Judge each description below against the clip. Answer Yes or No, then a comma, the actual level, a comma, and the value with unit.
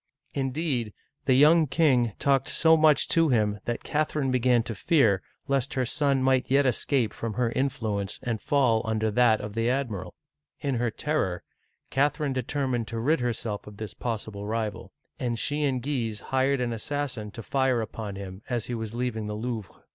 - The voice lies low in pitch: Yes, low, 125 Hz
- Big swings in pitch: No, average, 3.8 semitones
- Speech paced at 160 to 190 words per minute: Yes, average, 185 wpm